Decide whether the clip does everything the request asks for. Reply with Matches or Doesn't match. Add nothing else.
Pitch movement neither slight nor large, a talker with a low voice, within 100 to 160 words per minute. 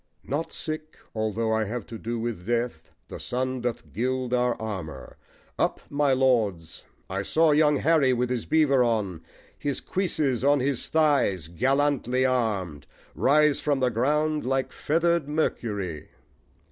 Matches